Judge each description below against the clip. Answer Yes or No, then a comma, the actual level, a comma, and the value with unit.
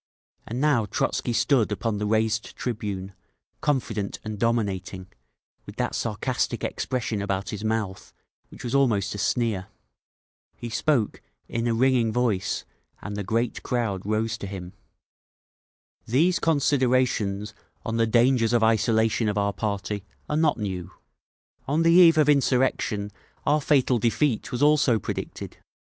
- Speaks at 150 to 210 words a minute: No, average, 140 wpm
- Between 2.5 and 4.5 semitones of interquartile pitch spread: Yes, average, 3.8 semitones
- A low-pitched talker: Yes, low, 115 Hz